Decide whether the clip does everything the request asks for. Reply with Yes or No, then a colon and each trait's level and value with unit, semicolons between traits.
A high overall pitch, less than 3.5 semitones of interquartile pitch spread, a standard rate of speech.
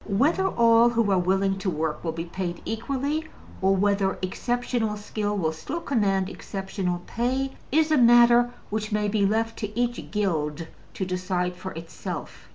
No: high, 205 Hz; average, 4.4 semitones; average, 165 wpm